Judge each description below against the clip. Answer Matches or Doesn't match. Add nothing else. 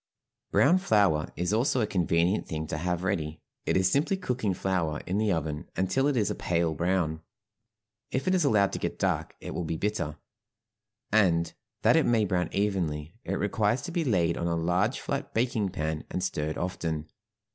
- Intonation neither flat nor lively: Matches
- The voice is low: Matches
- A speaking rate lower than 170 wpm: Doesn't match